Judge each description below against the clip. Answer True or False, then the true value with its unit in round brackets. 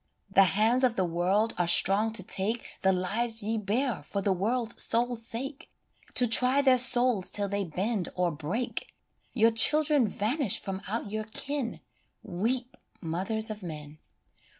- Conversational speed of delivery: True (155 wpm)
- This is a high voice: True (220 Hz)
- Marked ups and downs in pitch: False (4.1 semitones)